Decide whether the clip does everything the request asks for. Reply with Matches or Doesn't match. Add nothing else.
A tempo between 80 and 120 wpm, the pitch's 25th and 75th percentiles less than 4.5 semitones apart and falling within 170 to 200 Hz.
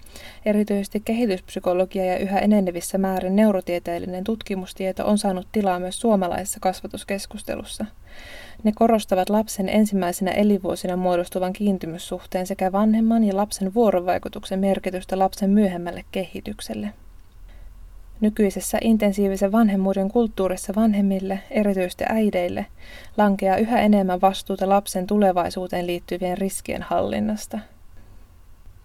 Matches